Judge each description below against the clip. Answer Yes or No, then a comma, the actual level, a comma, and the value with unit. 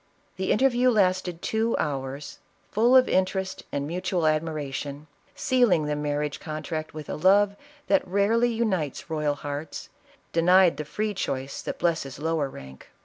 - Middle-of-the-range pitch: Yes, medium, 165 Hz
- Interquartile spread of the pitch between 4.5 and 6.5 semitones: Yes, wide, 5.4 semitones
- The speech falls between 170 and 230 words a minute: No, average, 145 wpm